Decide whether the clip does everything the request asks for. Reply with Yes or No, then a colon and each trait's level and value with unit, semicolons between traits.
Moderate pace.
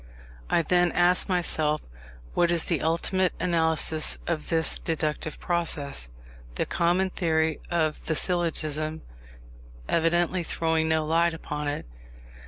No: slow, 120 wpm